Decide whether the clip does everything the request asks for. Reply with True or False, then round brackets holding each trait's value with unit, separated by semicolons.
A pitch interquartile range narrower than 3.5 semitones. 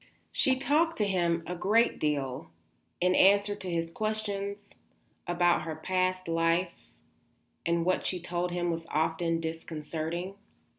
True (3.1 semitones)